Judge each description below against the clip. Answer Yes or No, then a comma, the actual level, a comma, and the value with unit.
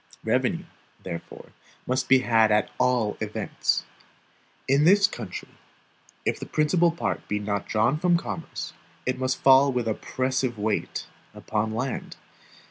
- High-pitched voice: No, low, 130 Hz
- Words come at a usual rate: No, slow, 130 wpm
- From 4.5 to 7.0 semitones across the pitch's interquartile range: Yes, average, 5.2 semitones